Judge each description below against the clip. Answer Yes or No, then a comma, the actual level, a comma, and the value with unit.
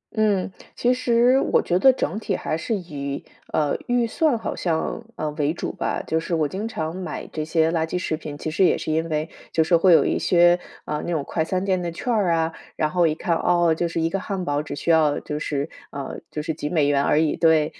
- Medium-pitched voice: Yes, medium, 165 Hz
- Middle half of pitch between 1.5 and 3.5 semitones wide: Yes, average, 3.2 semitones